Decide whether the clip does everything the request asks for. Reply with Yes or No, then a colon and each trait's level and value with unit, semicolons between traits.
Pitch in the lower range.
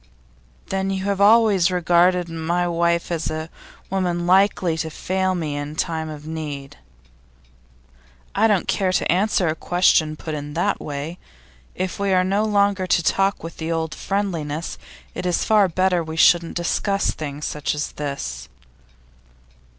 No: medium, 175 Hz